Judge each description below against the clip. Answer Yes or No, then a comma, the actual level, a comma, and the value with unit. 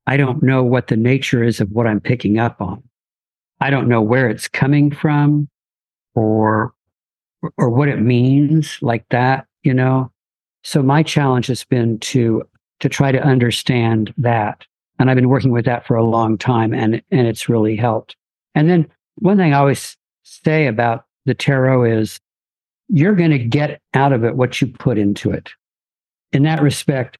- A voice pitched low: Yes, low, 125 Hz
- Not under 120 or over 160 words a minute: No, average, 180 wpm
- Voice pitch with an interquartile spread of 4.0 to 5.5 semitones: No, average, 3.6 semitones